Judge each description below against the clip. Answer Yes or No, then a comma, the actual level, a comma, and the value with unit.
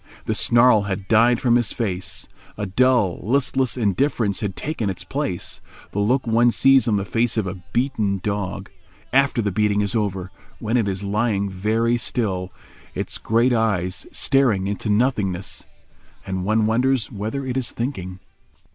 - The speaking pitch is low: Yes, low, 110 Hz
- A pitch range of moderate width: Yes, average, 3.6 semitones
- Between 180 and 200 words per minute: No, average, 155 wpm